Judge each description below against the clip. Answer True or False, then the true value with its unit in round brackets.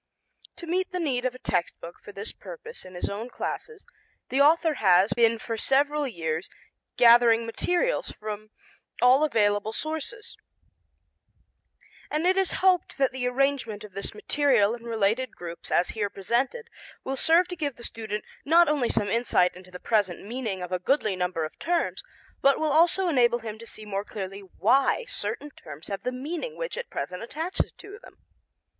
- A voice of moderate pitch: False (240 Hz)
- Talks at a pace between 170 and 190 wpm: True (175 wpm)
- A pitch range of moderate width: False (6.9 semitones)